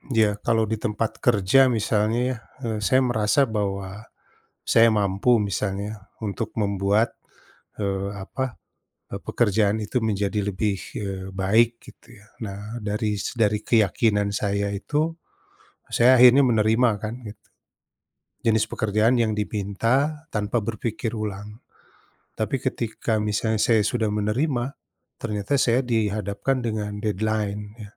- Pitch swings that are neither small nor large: No, narrow, 1.9 semitones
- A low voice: Yes, low, 105 Hz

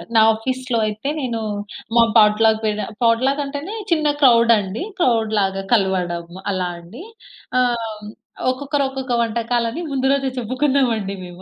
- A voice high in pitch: Yes, high, 230 Hz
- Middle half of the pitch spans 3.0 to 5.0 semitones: Yes, average, 3.8 semitones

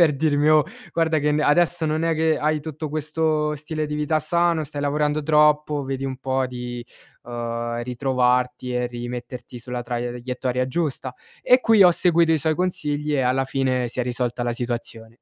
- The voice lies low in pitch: No, medium, 145 Hz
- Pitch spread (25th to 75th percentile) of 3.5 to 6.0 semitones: Yes, average, 3.8 semitones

